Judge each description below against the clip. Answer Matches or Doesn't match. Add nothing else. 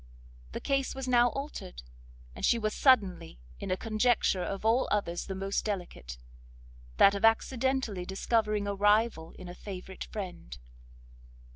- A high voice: Matches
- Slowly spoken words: Doesn't match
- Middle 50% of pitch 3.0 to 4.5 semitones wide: Matches